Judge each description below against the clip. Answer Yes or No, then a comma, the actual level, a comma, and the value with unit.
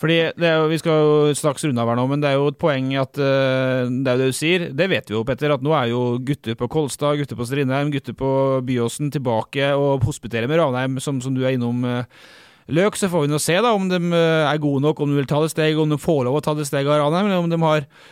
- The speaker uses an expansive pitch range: No, average, 3.1 semitones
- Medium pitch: Yes, medium, 145 Hz